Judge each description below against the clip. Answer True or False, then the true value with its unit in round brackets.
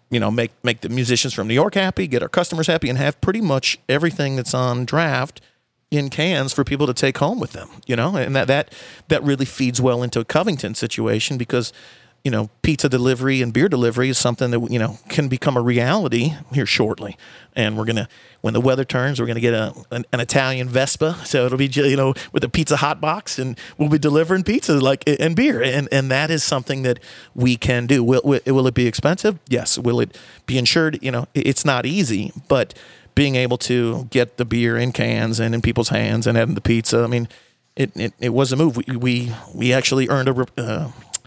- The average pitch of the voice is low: True (130 Hz)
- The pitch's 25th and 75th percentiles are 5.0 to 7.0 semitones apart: False (3.0 semitones)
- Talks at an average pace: False (220 wpm)